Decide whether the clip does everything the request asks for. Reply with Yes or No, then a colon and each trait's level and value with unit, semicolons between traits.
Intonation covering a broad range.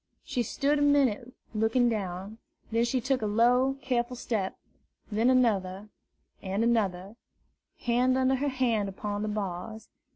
No: average, 3.6 semitones